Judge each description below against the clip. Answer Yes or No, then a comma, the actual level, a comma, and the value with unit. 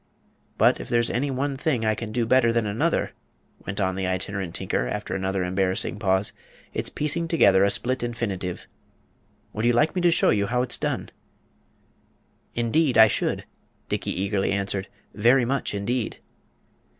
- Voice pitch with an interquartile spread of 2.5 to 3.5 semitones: No, average, 4.3 semitones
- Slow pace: No, average, 165 wpm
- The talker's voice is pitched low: Yes, low, 110 Hz